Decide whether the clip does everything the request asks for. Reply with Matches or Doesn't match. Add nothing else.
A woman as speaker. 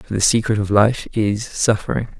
Doesn't match